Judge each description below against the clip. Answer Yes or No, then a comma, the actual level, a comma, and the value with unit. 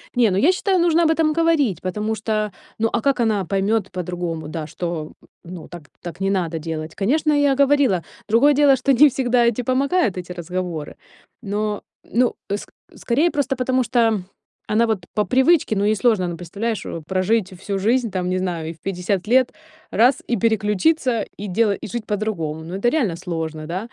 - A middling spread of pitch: No, wide, 5.8 semitones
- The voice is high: Yes, high, 210 Hz